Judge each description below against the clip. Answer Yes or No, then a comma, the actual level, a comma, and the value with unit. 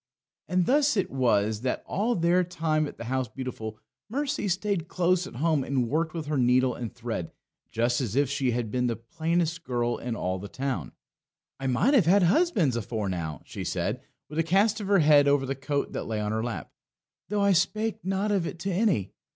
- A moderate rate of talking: No, fast, 210 wpm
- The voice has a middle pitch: Yes, medium, 145 Hz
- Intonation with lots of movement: Yes, wide, 7.2 semitones